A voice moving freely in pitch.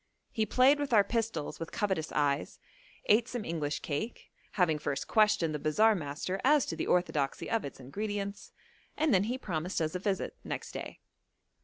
Yes: wide, 6.1 semitones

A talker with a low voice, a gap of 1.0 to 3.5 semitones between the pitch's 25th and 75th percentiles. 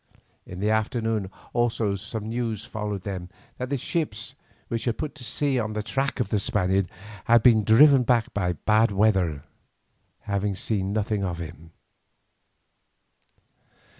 Yes: low, 110 Hz; average, 3.2 semitones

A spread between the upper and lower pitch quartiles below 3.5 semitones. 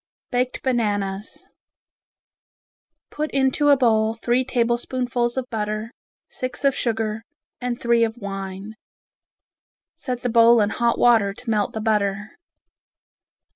Yes: average, 2.7 semitones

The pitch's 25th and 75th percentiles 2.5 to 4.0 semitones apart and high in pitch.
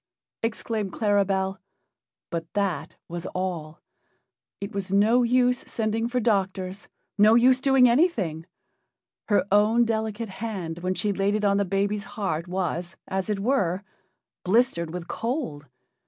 Yes: average, 3.6 semitones; high, 200 Hz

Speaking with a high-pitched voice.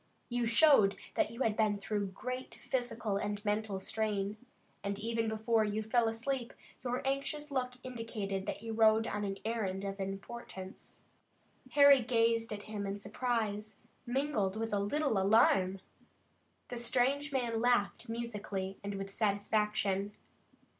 Yes: high, 220 Hz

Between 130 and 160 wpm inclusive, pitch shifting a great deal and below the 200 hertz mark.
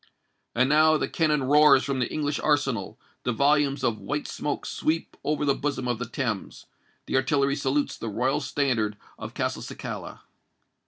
No: average, 155 wpm; average, 2.8 semitones; medium, 140 Hz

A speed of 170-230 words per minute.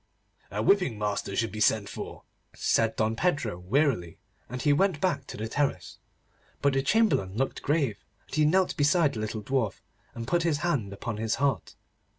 Yes: average, 180 wpm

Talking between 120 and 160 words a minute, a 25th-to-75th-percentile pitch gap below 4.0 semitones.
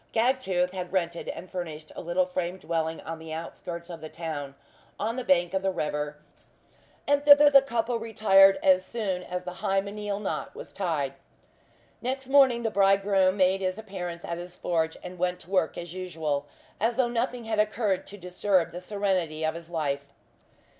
No: average, 180 wpm; average, 3.6 semitones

